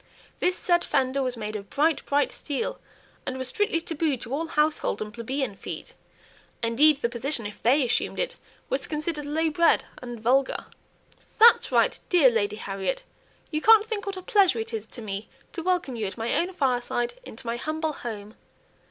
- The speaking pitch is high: Yes, very high, 275 Hz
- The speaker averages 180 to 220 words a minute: Yes, average, 185 wpm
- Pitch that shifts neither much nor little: No, wide, 5.9 semitones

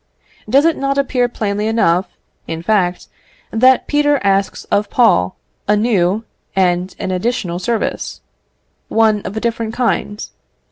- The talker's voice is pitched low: No, high, 215 Hz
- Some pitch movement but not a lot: Yes, average, 4.4 semitones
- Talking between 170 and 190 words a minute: No, slow, 135 wpm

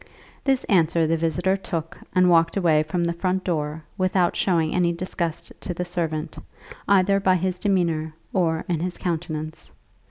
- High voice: No, medium, 170 Hz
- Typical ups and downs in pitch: No, narrow, 2.2 semitones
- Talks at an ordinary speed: Yes, average, 160 wpm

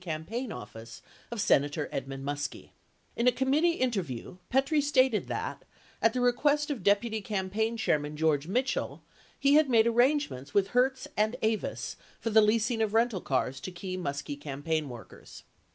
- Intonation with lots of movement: Yes, wide, 8.7 semitones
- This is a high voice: Yes, high, 215 Hz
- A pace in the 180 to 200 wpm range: No, average, 155 wpm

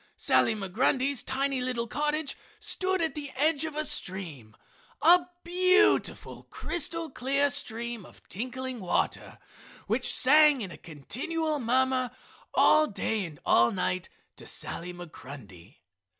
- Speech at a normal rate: No, slow, 125 wpm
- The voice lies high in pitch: Yes, very high, 260 Hz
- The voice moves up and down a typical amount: No, wide, 7.8 semitones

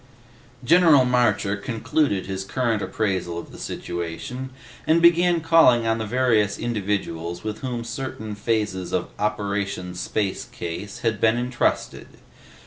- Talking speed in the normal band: No, slow, 130 wpm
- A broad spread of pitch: No, average, 4.2 semitones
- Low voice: Yes, low, 110 Hz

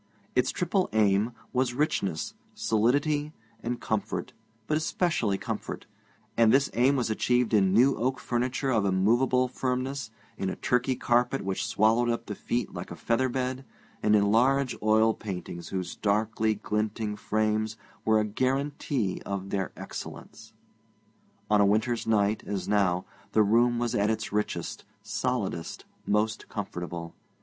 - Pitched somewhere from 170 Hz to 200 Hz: No, low, 110 Hz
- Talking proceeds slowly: No, average, 145 wpm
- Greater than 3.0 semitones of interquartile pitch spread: Yes, average, 3.6 semitones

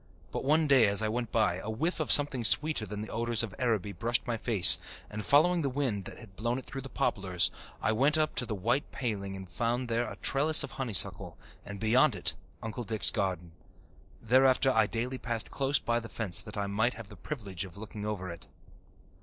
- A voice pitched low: Yes, low, 115 Hz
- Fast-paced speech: Yes, fast, 215 wpm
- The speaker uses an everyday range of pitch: Yes, average, 4.1 semitones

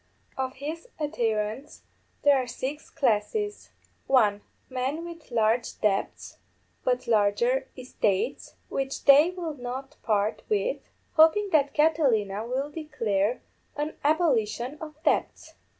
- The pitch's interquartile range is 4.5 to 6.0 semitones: Yes, average, 5.3 semitones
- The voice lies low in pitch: No, very high, 265 Hz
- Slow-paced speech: Yes, slow, 115 wpm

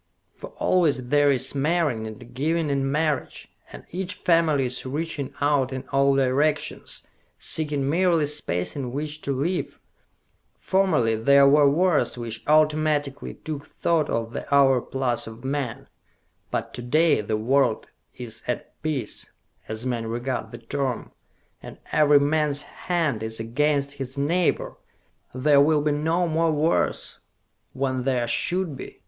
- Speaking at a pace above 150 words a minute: No, average, 140 wpm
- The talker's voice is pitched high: No, medium, 140 Hz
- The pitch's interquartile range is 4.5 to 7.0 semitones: No, average, 3.4 semitones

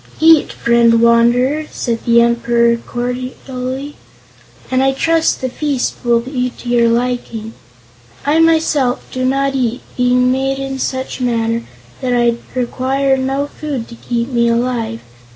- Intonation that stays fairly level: Yes, narrow, 2.3 semitones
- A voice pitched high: Yes, very high, 250 Hz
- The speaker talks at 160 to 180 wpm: No, average, 140 wpm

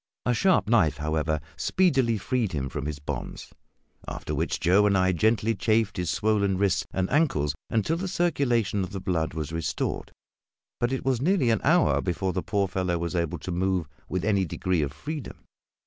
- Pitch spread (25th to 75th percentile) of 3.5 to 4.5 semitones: No, wide, 5.6 semitones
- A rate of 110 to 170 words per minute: No, average, 185 wpm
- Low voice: Yes, very low, 95 Hz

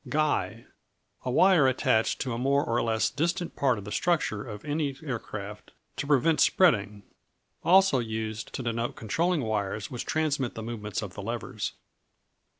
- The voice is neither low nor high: No, low, 125 Hz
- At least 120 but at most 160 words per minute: Yes, average, 155 wpm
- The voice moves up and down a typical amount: No, wide, 5.7 semitones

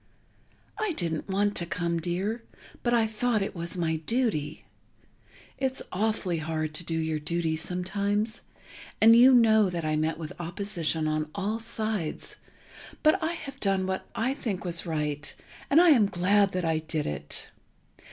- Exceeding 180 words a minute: No, average, 160 wpm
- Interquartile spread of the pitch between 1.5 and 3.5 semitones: No, wide, 5.4 semitones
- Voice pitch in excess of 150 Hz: Yes, medium, 185 Hz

